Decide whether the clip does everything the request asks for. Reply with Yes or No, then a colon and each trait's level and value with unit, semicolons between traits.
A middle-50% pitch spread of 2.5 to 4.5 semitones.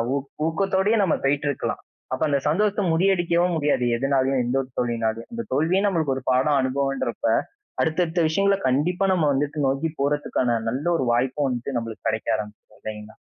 No: average, 4.9 semitones